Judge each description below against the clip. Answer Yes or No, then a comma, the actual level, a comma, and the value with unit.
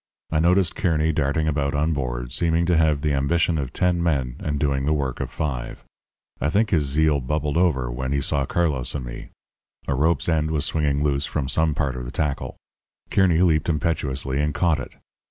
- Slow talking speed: No, average, 200 wpm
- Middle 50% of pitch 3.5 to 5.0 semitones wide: No, average, 2.8 semitones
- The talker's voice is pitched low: Yes, very low, 75 Hz